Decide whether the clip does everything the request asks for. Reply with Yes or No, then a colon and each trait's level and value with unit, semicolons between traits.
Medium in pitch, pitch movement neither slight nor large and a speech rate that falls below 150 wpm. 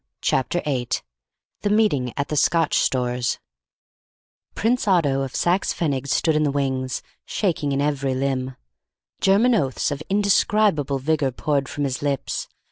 Yes: medium, 145 Hz; average, 4.6 semitones; average, 140 wpm